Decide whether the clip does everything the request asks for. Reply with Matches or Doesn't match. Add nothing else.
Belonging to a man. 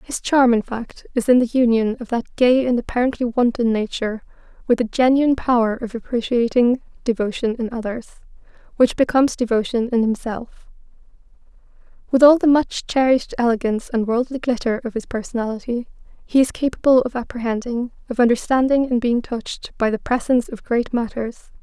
Doesn't match